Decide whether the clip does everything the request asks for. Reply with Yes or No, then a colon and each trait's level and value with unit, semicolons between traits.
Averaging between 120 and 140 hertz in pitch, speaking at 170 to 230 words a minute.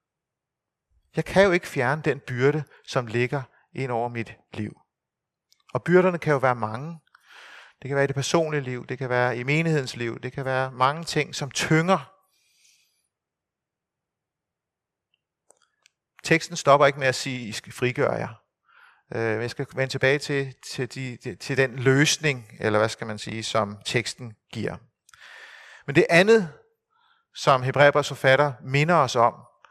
No: low, 135 Hz; average, 160 wpm